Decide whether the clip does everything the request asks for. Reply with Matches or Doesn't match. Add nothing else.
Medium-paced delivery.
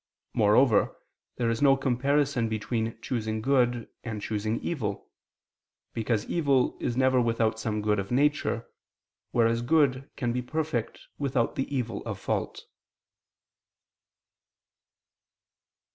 Doesn't match